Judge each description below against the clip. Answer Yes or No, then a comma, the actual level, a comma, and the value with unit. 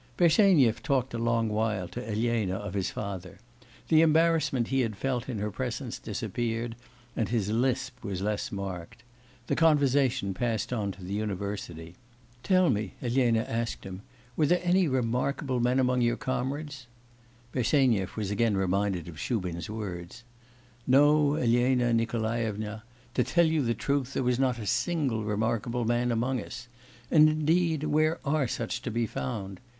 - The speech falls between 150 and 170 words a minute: Yes, average, 155 wpm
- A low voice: Yes, low, 120 Hz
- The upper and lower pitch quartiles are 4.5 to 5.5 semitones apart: No, average, 4.1 semitones